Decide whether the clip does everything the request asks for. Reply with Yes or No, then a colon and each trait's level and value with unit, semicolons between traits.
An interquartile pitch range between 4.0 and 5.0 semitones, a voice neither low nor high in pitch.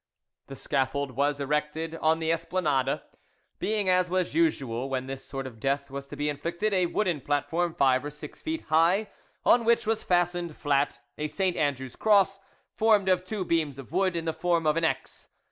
Yes: average, 4.7 semitones; medium, 160 Hz